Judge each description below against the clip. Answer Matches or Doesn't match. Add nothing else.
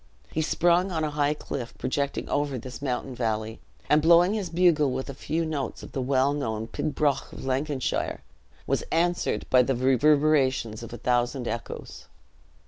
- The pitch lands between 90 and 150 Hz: Matches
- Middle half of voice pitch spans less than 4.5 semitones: Matches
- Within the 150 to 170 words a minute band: Matches